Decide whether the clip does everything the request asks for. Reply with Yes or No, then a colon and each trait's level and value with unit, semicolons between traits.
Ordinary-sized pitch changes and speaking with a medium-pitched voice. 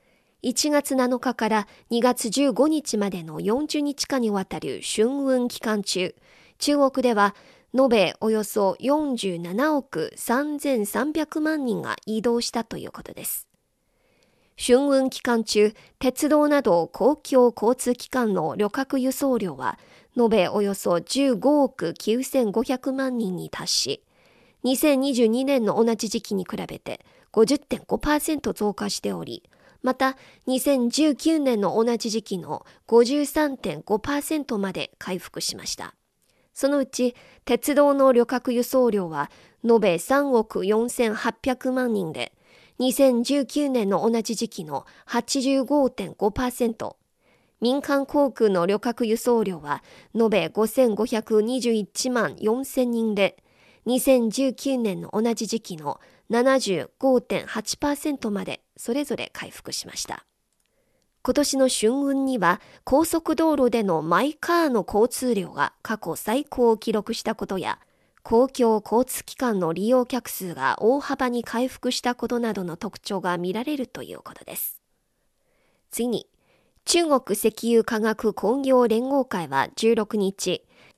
No: average, 3.9 semitones; high, 235 Hz